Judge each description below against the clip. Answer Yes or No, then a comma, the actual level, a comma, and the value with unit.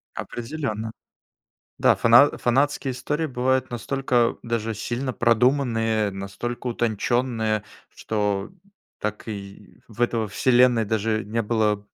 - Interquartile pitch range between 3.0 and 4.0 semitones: No, narrow, 2.6 semitones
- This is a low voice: Yes, low, 115 Hz